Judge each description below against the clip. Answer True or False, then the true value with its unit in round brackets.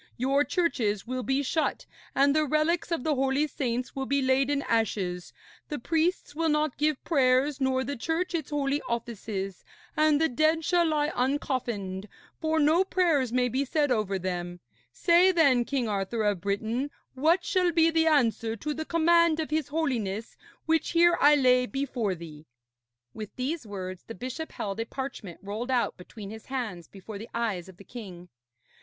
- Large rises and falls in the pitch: True (5.9 semitones)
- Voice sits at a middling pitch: False (265 Hz)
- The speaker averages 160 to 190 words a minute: True (175 wpm)